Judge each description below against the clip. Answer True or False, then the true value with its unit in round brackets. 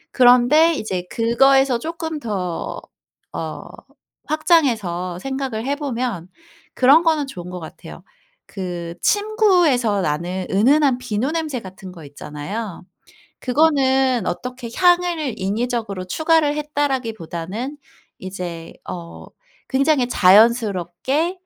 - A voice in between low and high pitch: False (245 Hz)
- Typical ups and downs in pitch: False (7.6 semitones)